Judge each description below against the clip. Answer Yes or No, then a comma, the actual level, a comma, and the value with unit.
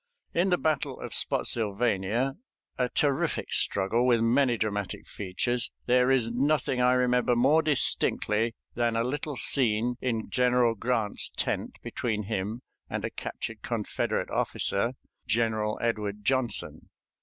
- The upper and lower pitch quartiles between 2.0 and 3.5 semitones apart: Yes, average, 2.7 semitones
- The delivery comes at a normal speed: No, slow, 130 wpm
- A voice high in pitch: No, low, 120 Hz